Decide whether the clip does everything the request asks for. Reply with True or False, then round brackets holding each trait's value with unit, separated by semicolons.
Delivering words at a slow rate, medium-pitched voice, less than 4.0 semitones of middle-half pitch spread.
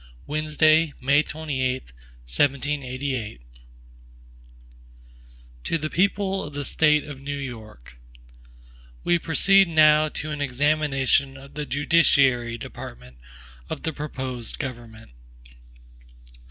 True (100 wpm; 145 Hz; 3.2 semitones)